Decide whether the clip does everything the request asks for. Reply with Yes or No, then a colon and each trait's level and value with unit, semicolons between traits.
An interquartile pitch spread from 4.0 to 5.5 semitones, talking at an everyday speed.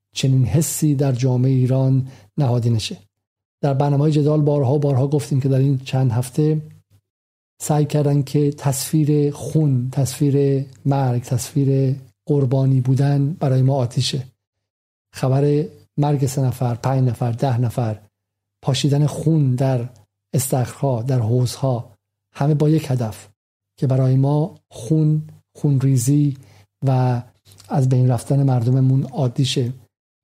No: average, 2.9 semitones; average, 120 wpm